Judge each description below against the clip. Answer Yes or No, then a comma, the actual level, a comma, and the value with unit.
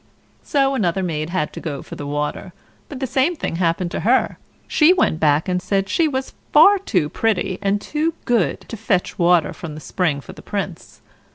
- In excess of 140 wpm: Yes, average, 200 wpm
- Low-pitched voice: No, high, 190 Hz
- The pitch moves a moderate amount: No, wide, 8.0 semitones